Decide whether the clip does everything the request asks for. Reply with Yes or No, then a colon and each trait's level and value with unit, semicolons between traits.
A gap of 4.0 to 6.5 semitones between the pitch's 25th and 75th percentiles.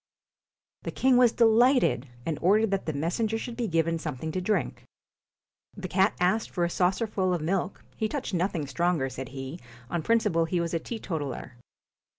Yes: average, 5.2 semitones